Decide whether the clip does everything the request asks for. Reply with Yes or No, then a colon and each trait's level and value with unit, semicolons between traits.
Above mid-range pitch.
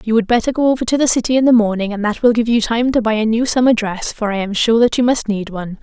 Yes: high, 225 Hz